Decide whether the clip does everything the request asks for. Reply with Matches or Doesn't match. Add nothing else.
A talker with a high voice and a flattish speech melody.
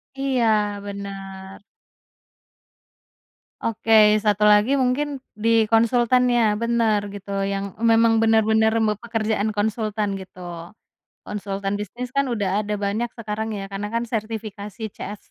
Matches